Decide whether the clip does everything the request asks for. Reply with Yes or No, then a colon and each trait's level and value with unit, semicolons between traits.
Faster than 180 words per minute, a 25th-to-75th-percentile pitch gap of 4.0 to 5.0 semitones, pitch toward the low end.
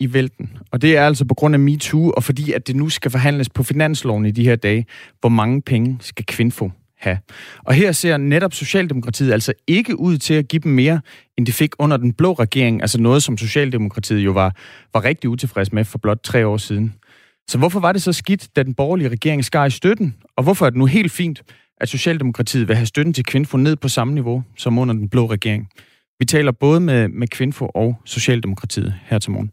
Yes: fast, 225 wpm; average, 4.5 semitones; low, 130 Hz